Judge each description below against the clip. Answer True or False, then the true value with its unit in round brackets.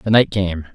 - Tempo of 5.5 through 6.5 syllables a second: False (4.9 syllables/s)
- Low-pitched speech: True (100 Hz)